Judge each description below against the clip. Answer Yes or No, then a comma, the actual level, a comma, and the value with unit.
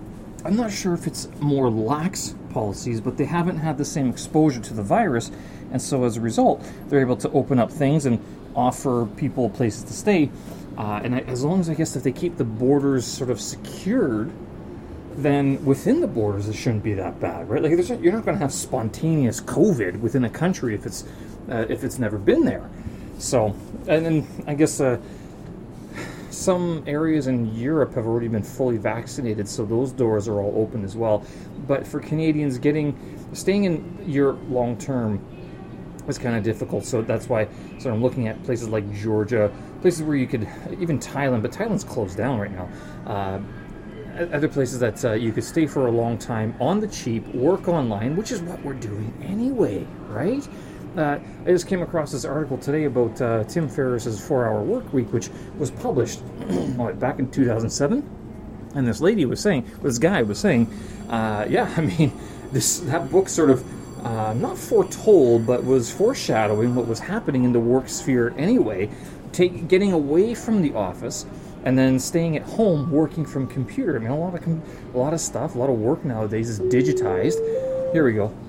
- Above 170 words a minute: Yes, average, 190 wpm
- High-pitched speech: No, low, 130 Hz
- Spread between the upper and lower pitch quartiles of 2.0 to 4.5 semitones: No, wide, 5.4 semitones